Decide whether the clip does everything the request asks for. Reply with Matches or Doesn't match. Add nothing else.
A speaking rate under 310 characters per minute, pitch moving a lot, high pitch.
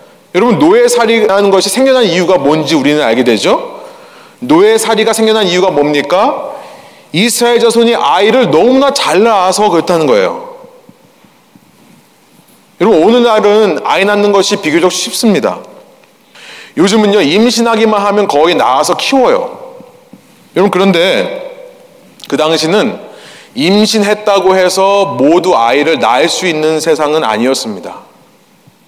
Matches